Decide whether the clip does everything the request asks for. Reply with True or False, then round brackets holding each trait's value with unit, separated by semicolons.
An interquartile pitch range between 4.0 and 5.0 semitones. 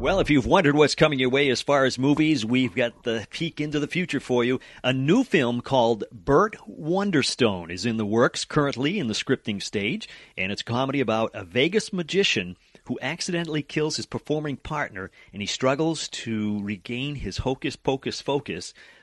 True (4.6 semitones)